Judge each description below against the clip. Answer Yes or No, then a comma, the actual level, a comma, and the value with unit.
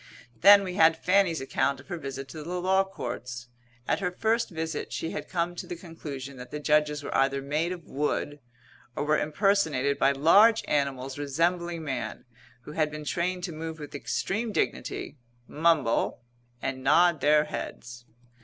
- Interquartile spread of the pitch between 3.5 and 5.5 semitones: Yes, average, 3.9 semitones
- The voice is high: No, medium, 155 Hz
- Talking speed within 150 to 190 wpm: Yes, average, 170 wpm